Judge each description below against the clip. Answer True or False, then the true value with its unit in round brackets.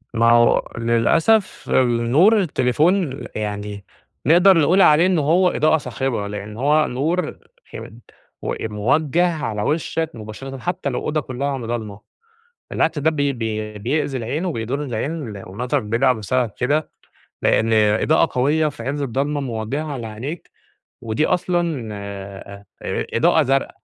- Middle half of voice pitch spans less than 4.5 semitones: False (5.6 semitones)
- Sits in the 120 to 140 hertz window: True (135 Hz)